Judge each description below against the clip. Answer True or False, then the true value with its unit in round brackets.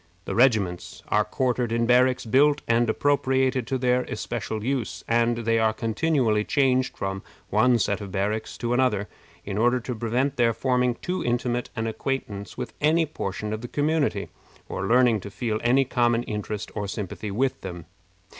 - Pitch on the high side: False (120 Hz)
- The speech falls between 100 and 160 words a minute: False (170 wpm)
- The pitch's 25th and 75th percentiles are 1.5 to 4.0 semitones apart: True (3.2 semitones)